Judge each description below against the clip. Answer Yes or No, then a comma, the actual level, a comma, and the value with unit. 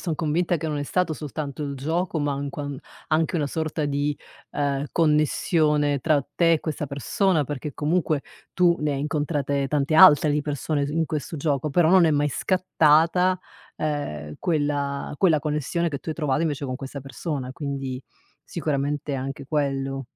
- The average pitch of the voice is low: No, medium, 150 Hz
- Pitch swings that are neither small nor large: No, narrow, 2.2 semitones